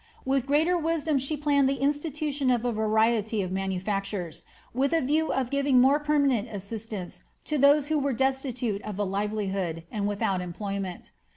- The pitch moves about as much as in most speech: No, wide, 5.7 semitones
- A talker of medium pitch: No, high, 245 Hz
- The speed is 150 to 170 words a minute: Yes, average, 165 wpm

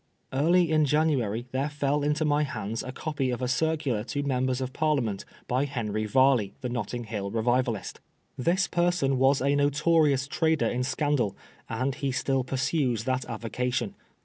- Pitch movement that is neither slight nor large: Yes, average, 3.3 semitones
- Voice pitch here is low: Yes, low, 130 Hz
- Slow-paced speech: No, average, 160 wpm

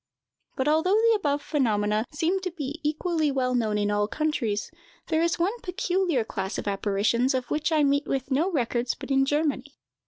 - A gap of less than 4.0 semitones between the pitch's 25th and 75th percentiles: No, average, 5.2 semitones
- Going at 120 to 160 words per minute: No, average, 185 wpm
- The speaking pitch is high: Yes, very high, 285 Hz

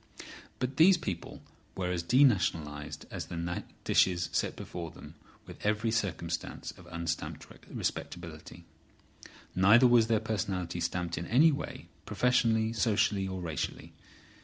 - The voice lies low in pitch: Yes, very low, 95 Hz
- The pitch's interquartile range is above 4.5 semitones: Yes, average, 4.9 semitones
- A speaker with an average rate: No, slow, 125 wpm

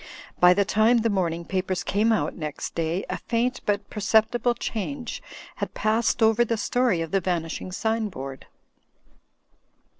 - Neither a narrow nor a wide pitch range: Yes, average, 4.3 semitones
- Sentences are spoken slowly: No, average, 150 wpm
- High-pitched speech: Yes, high, 210 Hz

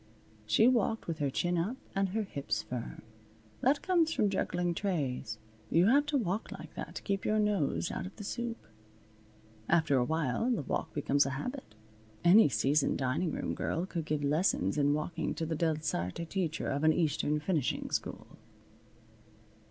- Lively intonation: Yes, wide, 5.9 semitones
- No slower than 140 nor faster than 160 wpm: No, average, 170 wpm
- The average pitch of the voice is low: No, medium, 170 Hz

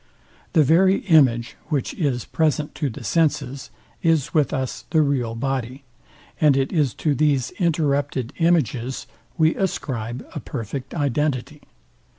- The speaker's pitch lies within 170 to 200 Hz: No, medium, 140 Hz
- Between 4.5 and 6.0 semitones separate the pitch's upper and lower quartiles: No, average, 3.7 semitones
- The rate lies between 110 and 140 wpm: Yes, slow, 135 wpm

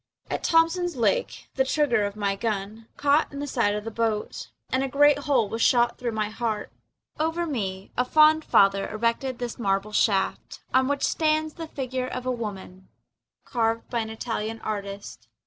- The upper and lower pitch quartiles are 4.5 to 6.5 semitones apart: Yes, average, 5.1 semitones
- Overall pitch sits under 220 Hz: No, high, 235 Hz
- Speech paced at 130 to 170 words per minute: No, average, 180 wpm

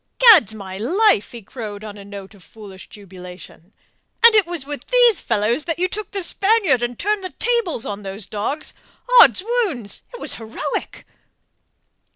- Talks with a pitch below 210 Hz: No, high, 240 Hz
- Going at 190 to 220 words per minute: No, average, 165 wpm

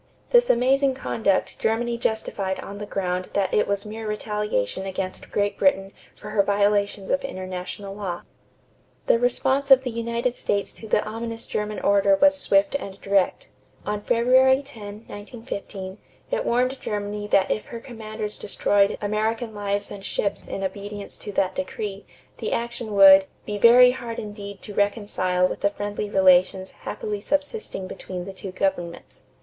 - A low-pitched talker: No, high, 205 Hz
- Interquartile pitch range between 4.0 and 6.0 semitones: No, average, 3.0 semitones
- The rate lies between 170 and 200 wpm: No, average, 155 wpm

